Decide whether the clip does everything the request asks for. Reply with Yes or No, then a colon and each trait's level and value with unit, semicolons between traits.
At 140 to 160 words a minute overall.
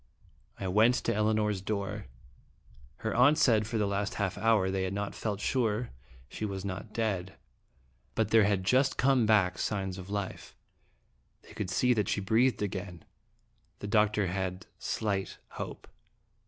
Yes: average, 155 wpm